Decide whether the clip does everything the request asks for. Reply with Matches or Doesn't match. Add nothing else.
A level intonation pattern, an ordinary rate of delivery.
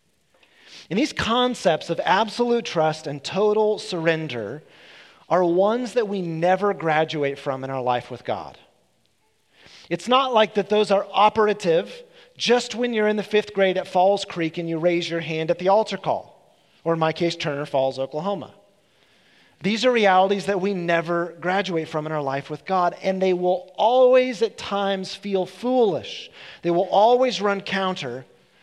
Doesn't match